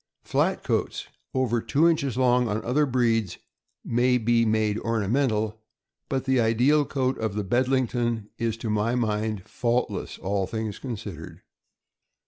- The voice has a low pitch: Yes, low, 115 Hz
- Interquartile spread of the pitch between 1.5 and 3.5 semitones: Yes, average, 2.9 semitones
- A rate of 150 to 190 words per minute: No, average, 140 wpm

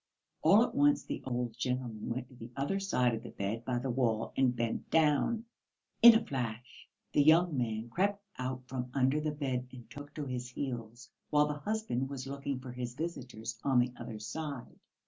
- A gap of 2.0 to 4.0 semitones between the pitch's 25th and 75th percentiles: Yes, average, 3.5 semitones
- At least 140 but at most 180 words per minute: No, average, 195 wpm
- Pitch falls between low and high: No, low, 130 Hz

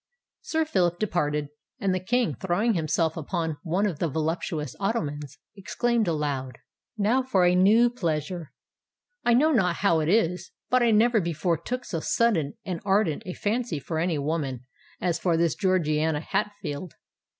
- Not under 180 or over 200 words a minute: No, average, 160 wpm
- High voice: No, medium, 175 Hz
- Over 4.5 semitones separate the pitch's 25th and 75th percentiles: Yes, average, 5.0 semitones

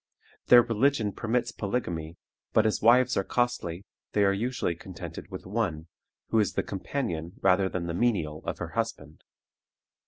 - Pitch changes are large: Yes, wide, 5.7 semitones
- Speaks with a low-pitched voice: Yes, low, 100 Hz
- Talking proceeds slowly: No, average, 155 wpm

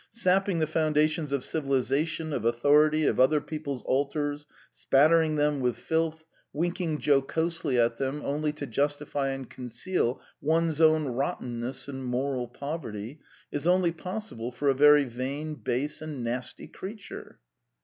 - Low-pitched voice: No, medium, 145 Hz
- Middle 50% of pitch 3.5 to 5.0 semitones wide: No, average, 3.1 semitones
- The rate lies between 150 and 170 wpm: No, average, 140 wpm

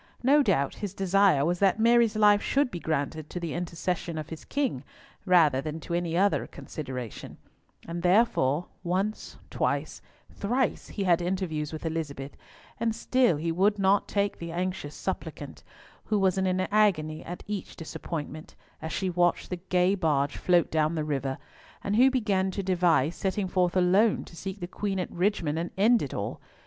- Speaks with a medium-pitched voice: Yes, medium, 180 Hz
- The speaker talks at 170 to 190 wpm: Yes, average, 175 wpm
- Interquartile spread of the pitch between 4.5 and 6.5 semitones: No, average, 3.9 semitones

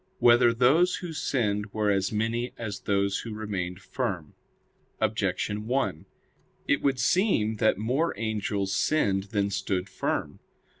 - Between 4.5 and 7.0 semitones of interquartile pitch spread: No, average, 3.8 semitones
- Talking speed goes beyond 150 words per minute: No, average, 140 wpm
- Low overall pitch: Yes, low, 105 Hz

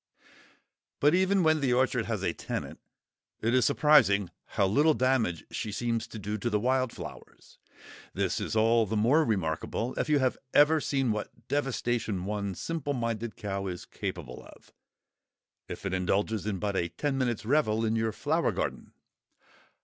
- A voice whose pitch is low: Yes, low, 115 Hz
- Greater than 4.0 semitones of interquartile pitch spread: Yes, average, 4.5 semitones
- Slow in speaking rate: No, average, 165 wpm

